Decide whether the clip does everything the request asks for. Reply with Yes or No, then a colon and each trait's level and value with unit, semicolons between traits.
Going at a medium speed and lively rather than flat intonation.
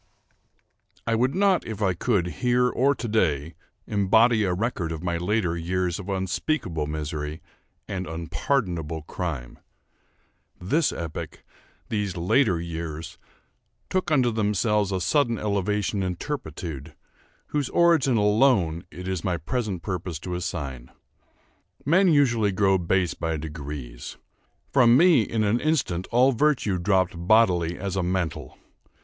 No: slow, 130 wpm; wide, 5.7 semitones